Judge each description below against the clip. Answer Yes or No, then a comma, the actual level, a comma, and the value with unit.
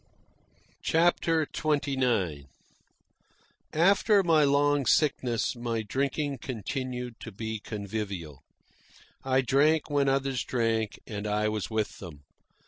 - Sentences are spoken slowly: Yes, slow, 105 wpm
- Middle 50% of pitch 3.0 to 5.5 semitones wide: Yes, average, 5.1 semitones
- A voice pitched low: Yes, low, 125 Hz